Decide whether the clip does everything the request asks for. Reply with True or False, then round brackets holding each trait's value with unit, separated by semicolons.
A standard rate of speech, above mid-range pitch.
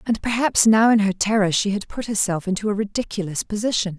False (210 wpm; 205 Hz)